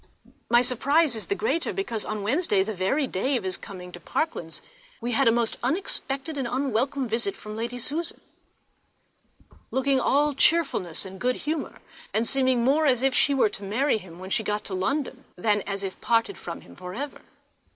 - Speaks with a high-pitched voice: Yes, high, 245 Hz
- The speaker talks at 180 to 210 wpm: Yes, average, 190 wpm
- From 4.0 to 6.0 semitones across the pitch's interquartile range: Yes, average, 5.2 semitones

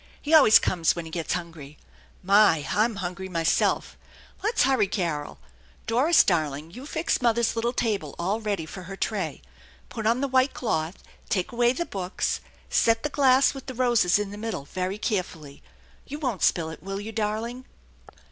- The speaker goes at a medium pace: Yes, average, 175 wpm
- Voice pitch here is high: Yes, high, 210 Hz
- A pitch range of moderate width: No, wide, 5.8 semitones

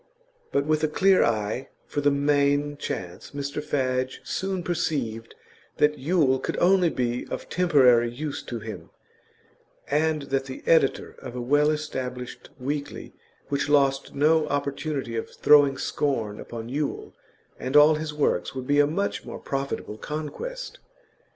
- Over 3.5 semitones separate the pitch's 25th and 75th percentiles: No, average, 2.9 semitones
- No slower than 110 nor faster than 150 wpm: Yes, average, 145 wpm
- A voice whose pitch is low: No, medium, 145 Hz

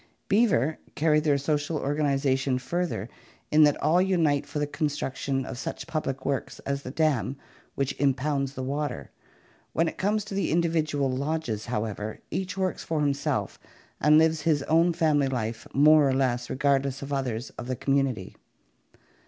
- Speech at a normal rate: Yes, average, 165 wpm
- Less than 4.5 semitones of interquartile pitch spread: Yes, average, 2.8 semitones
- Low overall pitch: No, medium, 145 Hz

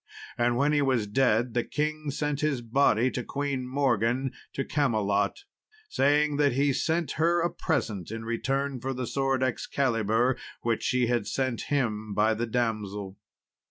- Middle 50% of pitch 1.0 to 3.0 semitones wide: No, average, 3.8 semitones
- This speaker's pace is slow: No, average, 160 wpm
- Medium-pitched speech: No, low, 125 Hz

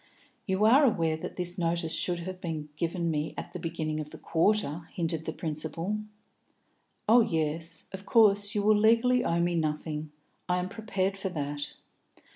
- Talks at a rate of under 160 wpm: No, average, 170 wpm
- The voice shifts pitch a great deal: No, average, 4.1 semitones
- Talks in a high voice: No, medium, 170 Hz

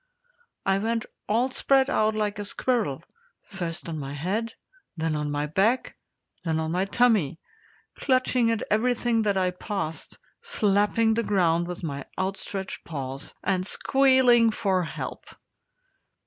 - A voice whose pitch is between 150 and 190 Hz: No, high, 200 Hz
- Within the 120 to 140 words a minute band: Yes, slow, 135 wpm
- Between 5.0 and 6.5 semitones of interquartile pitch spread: Yes, wide, 5.5 semitones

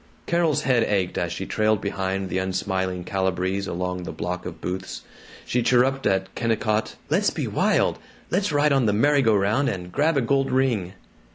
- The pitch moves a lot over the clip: Yes, wide, 5.9 semitones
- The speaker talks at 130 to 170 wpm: No, average, 180 wpm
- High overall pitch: No, low, 105 Hz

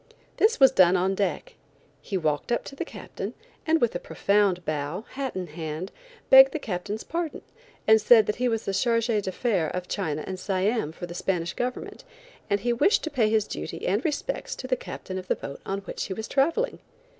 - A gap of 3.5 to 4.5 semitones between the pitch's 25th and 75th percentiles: No, wide, 5.4 semitones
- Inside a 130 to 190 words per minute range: No, average, 200 wpm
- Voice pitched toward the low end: No, high, 205 Hz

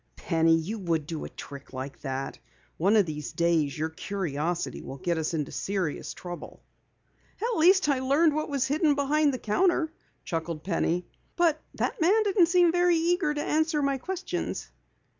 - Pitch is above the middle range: Yes, high, 220 Hz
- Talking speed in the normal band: Yes, average, 170 wpm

